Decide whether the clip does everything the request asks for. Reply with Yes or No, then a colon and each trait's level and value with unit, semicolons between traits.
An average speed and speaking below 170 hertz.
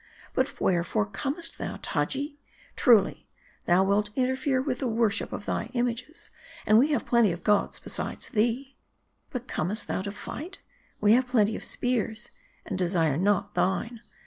No: average, 155 wpm; high, 225 Hz